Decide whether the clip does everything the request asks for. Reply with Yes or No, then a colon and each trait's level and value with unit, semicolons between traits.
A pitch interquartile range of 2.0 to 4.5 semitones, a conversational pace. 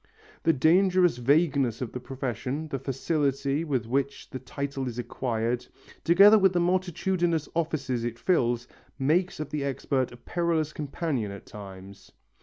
No: average, 5.2 semitones; average, 145 wpm